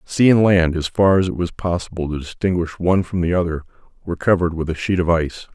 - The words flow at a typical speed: No, fast, 240 wpm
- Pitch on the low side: Yes, very low, 85 Hz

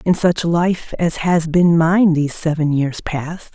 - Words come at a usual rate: Yes, average, 185 wpm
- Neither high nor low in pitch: Yes, medium, 165 Hz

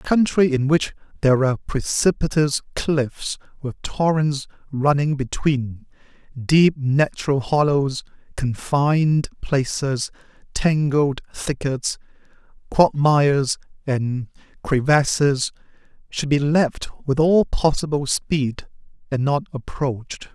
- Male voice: Yes, male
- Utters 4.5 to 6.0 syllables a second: No, 3.6 syllables/s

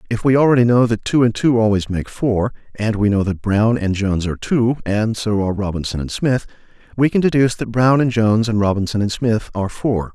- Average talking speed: No, fast, 230 wpm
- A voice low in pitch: Yes, low, 110 Hz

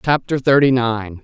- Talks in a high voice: No, low, 125 Hz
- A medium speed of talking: Yes, average, 145 wpm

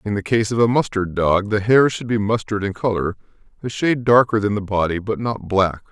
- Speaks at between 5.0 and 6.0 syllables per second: Yes, 5.5 syllables/s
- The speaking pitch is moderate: No, low, 105 Hz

